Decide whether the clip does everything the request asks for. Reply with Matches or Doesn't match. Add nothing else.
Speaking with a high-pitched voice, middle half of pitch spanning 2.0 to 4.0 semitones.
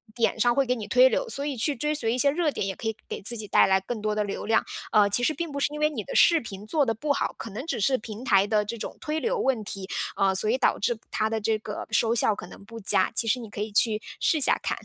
Doesn't match